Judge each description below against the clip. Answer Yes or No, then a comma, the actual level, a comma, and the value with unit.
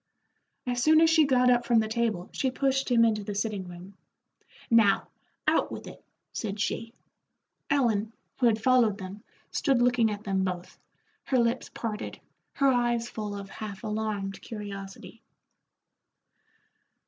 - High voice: Yes, high, 225 Hz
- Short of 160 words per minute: Yes, average, 150 wpm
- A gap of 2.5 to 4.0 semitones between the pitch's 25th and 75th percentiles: Yes, average, 3.3 semitones